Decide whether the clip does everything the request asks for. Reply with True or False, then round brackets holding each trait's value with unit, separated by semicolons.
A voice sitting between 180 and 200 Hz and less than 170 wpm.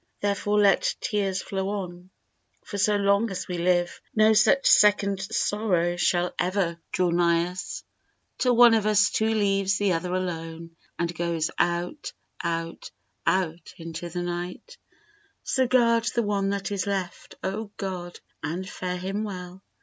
True (190 Hz; 150 wpm)